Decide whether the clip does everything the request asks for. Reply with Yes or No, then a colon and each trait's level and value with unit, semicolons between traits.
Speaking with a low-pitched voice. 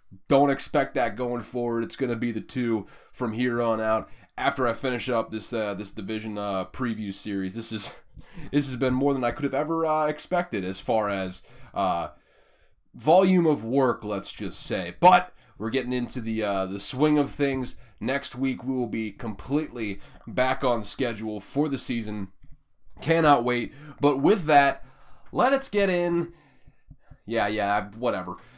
Yes: low, 120 Hz